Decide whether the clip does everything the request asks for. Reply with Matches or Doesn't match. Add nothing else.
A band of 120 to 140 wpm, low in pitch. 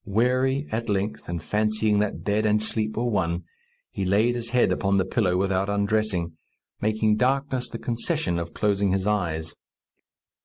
Doesn't match